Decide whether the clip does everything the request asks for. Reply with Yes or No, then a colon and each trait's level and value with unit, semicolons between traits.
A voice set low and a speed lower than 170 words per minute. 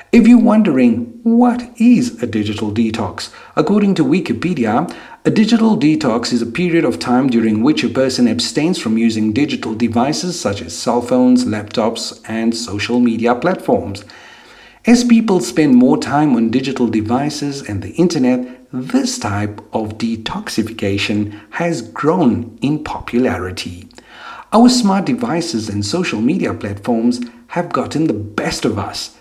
Yes: low, 130 Hz; average, 140 wpm